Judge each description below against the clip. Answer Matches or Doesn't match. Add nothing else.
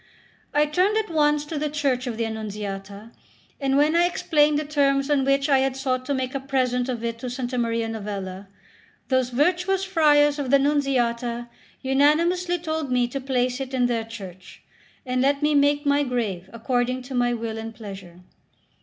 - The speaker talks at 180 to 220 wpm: Matches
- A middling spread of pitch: Matches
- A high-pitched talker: Matches